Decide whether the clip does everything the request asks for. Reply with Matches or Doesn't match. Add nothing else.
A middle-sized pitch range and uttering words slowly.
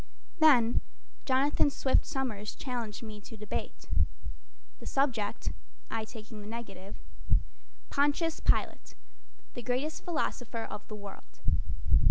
Matches